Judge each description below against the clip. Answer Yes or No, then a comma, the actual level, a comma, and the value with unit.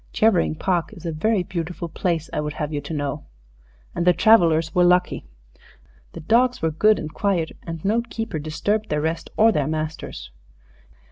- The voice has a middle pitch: Yes, medium, 165 Hz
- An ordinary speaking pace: Yes, average, 180 wpm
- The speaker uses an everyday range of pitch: Yes, average, 4.6 semitones